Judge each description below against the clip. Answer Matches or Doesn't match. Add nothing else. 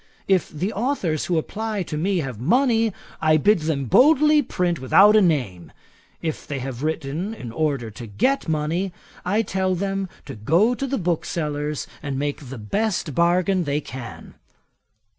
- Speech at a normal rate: Matches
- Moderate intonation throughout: Doesn't match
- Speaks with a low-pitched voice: Doesn't match